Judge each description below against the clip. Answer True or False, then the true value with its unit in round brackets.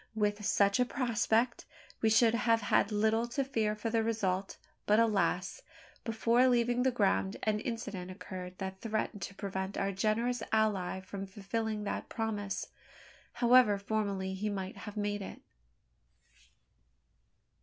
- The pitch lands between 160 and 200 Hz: False (210 Hz)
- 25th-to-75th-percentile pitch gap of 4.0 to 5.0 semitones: False (2.5 semitones)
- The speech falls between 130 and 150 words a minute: True (140 wpm)